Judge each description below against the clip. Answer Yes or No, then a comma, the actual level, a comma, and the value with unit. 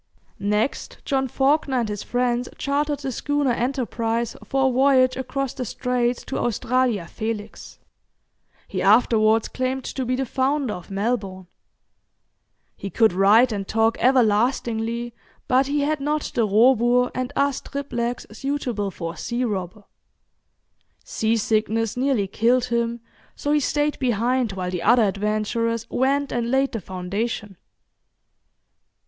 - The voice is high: Yes, high, 240 Hz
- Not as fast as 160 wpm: Yes, slow, 135 wpm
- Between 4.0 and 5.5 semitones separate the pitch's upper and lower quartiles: No, average, 3.4 semitones